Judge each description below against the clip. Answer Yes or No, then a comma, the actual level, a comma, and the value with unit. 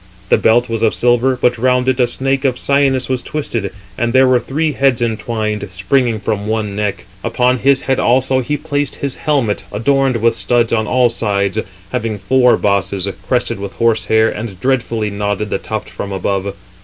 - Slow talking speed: No, average, 185 wpm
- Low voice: Yes, low, 120 Hz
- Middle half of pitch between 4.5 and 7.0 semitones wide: No, average, 3.6 semitones